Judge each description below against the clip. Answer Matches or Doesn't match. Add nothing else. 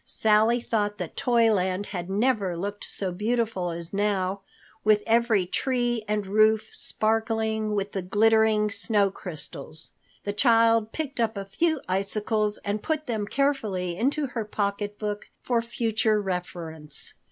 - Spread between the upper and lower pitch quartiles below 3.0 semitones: Matches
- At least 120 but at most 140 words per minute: Matches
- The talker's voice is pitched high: Matches